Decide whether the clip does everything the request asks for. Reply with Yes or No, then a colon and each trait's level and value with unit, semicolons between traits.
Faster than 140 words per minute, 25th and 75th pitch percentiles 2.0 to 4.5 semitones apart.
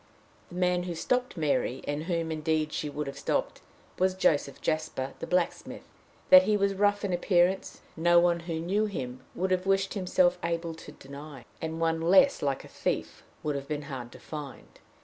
Yes: average, 190 wpm; average, 3.6 semitones